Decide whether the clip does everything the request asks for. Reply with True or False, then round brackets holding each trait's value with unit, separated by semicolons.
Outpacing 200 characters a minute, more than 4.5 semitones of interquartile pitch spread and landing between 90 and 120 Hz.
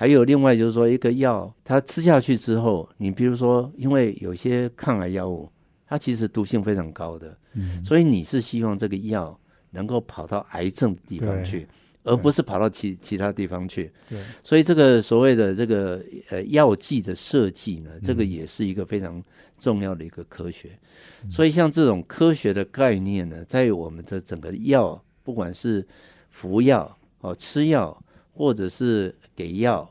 True (265 characters per minute; 5.1 semitones; 105 Hz)